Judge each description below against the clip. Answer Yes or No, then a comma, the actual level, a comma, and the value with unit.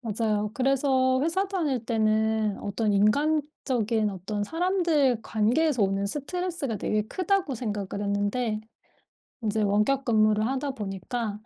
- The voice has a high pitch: Yes, high, 225 Hz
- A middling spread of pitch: Yes, average, 4.8 semitones